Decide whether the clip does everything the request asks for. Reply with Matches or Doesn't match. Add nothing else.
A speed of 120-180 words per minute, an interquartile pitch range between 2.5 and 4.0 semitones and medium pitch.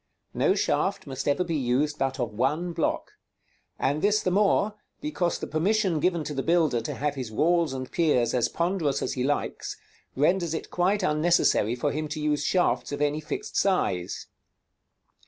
Doesn't match